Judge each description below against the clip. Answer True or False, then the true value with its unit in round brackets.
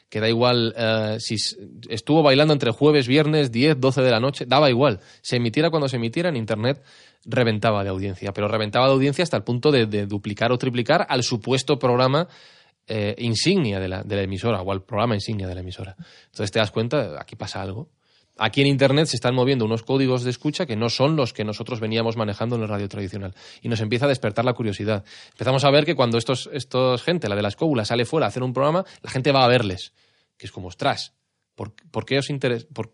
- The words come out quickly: True (230 wpm)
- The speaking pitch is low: True (120 Hz)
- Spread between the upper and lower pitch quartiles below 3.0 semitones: False (4.1 semitones)